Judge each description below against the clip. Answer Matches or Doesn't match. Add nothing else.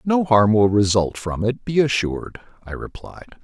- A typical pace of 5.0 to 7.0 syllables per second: Doesn't match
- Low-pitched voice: Matches